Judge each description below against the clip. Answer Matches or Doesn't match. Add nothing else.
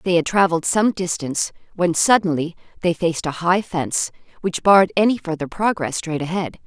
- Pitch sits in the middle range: Matches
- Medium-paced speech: Matches